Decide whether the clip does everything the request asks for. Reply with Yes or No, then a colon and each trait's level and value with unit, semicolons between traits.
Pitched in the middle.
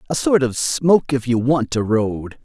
No: low, 130 Hz